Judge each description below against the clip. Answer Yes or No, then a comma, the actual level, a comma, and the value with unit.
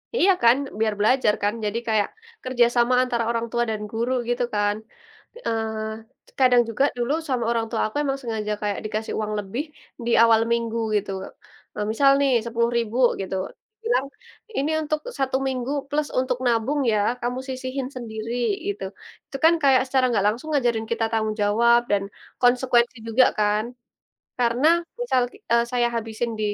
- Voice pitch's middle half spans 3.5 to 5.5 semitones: No, average, 2.7 semitones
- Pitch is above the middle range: Yes, high, 235 Hz